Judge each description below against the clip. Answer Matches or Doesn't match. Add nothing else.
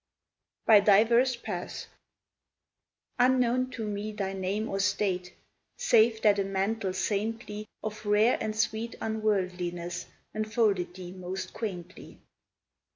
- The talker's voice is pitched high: Matches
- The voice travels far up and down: Doesn't match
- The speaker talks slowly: Matches